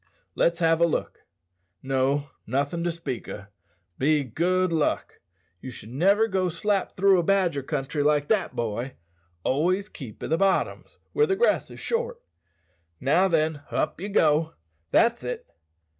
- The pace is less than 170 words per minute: Yes, average, 155 wpm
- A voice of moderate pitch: Yes, medium, 165 Hz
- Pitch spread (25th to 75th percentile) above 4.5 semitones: Yes, average, 5.3 semitones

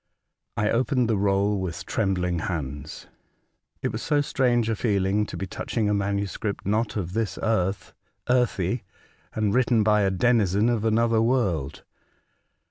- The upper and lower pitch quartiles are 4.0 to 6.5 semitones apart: No, average, 3.1 semitones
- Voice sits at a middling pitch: No, low, 105 Hz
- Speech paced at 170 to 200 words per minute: No, average, 150 wpm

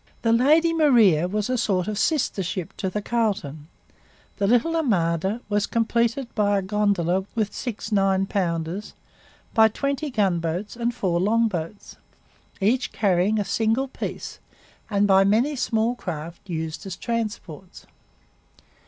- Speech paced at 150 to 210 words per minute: No, slow, 135 wpm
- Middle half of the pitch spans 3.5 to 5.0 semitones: Yes, average, 4.0 semitones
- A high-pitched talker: Yes, high, 210 Hz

